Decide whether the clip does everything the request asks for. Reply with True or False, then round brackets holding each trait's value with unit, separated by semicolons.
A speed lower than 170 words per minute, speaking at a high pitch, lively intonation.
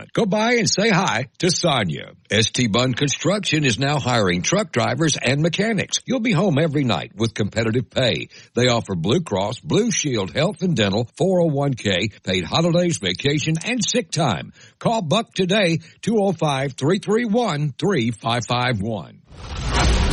False (140 wpm; 150 Hz; 7.7 semitones)